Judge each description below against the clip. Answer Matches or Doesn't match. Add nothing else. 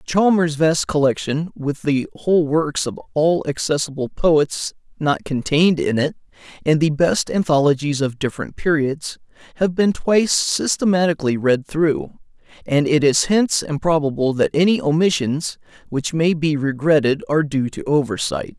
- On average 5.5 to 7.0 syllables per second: Doesn't match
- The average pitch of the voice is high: Doesn't match